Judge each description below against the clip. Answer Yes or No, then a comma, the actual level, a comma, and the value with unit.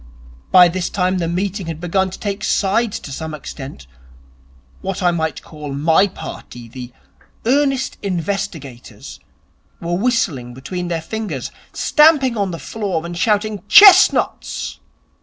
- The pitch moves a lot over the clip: No, average, 4.6 semitones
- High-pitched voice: No, medium, 180 Hz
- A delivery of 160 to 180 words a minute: No, slow, 135 wpm